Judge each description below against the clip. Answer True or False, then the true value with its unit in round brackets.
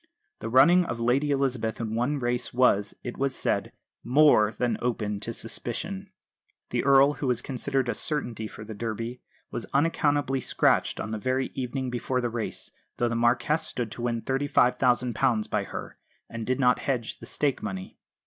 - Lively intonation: False (2.8 semitones)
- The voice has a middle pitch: False (125 Hz)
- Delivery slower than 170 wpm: False (175 wpm)